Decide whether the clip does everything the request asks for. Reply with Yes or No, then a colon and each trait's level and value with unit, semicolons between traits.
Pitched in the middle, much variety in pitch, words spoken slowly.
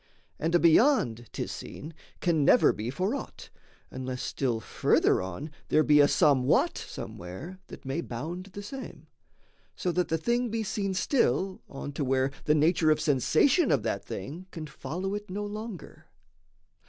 No: medium, 160 Hz; wide, 6.1 semitones; average, 165 wpm